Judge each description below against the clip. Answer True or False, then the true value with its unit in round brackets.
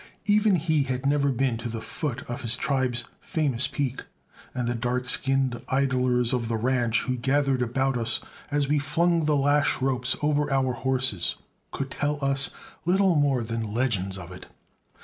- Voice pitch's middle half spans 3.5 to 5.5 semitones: False (3.0 semitones)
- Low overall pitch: True (130 Hz)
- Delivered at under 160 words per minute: False (170 wpm)